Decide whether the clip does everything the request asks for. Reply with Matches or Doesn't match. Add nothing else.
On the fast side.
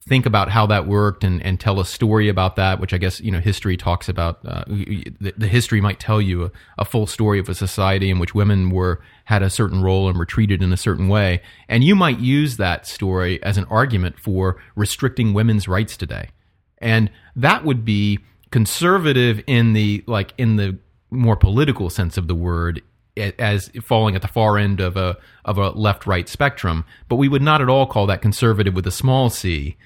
Matches